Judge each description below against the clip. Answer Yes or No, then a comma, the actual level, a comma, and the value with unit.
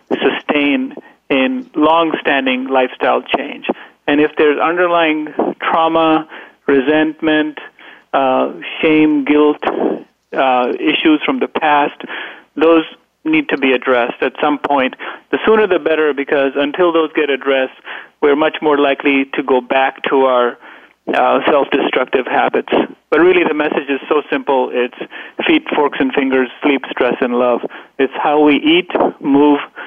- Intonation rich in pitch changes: No, average, 3.3 semitones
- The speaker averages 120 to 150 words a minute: Yes, average, 140 wpm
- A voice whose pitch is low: No, medium, 150 Hz